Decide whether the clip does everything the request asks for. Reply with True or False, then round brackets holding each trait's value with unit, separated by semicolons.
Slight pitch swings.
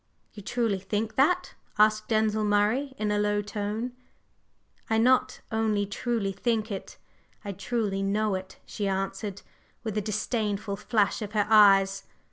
True (1.9 semitones)